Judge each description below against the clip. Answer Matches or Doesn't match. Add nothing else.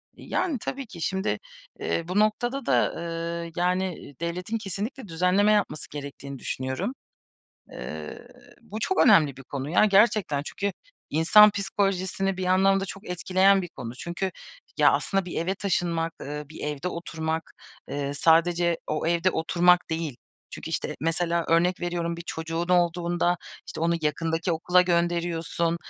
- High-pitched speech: Doesn't match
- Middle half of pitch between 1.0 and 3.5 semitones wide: Matches